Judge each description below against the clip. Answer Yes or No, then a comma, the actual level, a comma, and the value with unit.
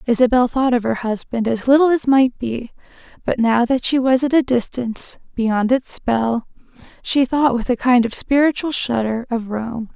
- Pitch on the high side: Yes, high, 245 Hz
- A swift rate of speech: No, average, 185 wpm